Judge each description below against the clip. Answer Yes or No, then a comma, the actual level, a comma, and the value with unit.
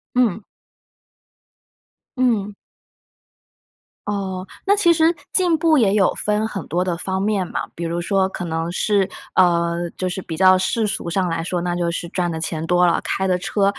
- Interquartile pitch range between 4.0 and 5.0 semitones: No, average, 3.2 semitones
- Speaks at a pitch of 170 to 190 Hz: Yes, medium, 185 Hz